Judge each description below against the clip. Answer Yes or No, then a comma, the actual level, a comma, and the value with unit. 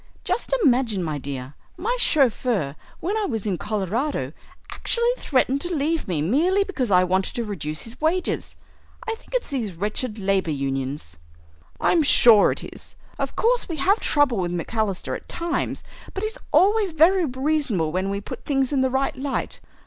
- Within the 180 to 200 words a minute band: No, average, 170 wpm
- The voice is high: Yes, very high, 250 Hz